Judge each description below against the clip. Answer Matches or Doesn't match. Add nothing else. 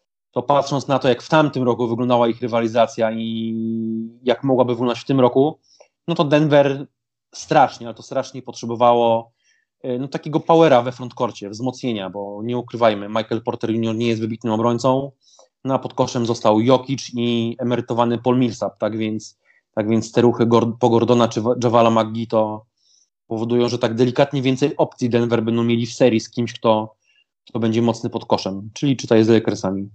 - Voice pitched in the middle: Doesn't match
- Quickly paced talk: Matches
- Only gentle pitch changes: Matches